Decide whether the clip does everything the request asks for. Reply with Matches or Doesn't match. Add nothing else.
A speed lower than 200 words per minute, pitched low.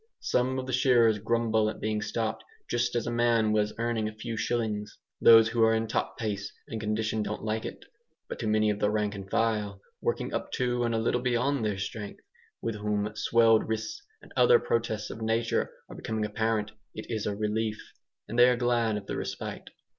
Doesn't match